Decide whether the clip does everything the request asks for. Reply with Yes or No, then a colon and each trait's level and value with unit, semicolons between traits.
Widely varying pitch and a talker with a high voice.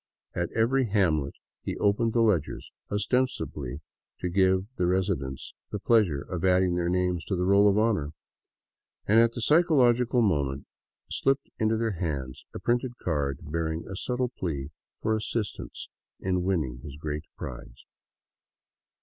No: wide, 6.0 semitones; very low, 95 Hz